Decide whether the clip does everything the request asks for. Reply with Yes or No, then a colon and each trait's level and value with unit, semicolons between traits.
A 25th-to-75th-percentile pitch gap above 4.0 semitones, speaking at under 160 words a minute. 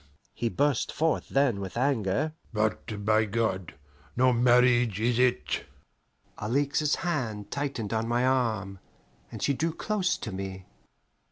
Yes: average, 4.5 semitones; slow, 135 wpm